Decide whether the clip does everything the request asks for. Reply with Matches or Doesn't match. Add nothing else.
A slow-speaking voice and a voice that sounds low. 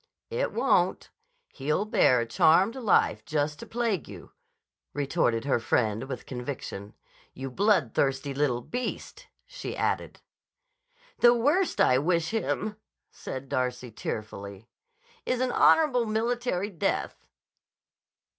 Doesn't match